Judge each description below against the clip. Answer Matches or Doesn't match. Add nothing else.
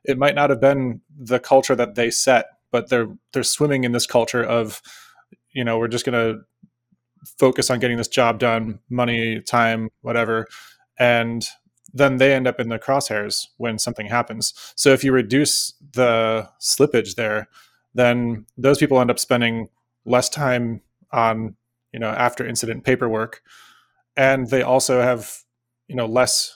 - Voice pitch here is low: Matches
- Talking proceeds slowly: Doesn't match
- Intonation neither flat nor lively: Doesn't match